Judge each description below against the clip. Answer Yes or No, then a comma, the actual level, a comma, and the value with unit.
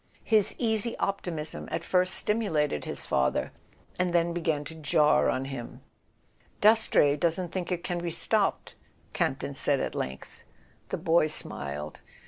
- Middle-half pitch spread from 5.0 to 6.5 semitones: No, average, 3.8 semitones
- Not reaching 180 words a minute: Yes, average, 150 wpm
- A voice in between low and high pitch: Yes, medium, 170 Hz